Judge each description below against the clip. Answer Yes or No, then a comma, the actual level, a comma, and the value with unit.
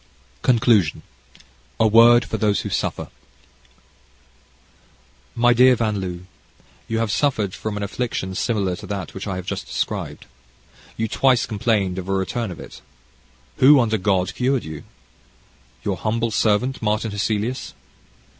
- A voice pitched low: Yes, low, 110 Hz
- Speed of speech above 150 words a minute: No, average, 140 wpm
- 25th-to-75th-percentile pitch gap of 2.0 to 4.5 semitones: Yes, average, 3.3 semitones